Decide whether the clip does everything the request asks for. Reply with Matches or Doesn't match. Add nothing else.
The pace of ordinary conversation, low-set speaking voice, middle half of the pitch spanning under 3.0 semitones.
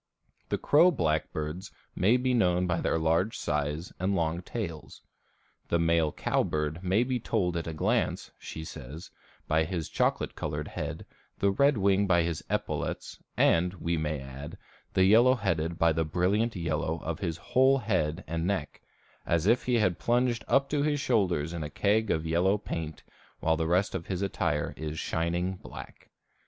Doesn't match